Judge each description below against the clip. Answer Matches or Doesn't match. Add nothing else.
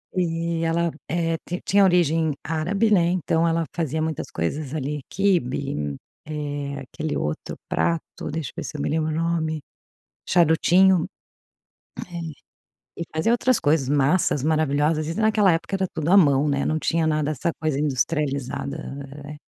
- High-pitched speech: Doesn't match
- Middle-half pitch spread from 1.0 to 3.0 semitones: Matches